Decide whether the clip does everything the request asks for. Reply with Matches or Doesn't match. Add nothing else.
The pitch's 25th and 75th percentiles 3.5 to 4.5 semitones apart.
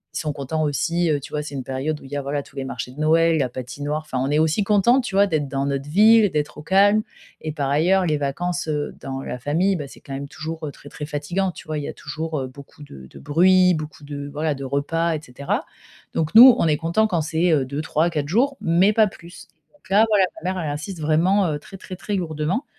Matches